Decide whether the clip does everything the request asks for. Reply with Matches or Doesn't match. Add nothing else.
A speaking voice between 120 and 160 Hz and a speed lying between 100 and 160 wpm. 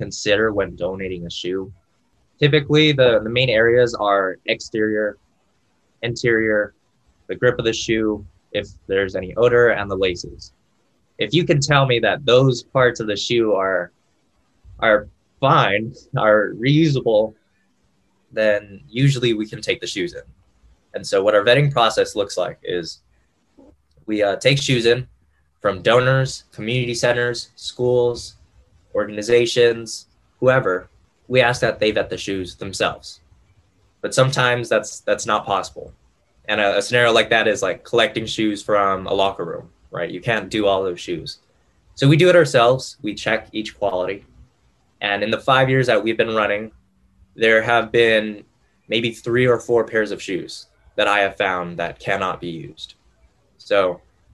Doesn't match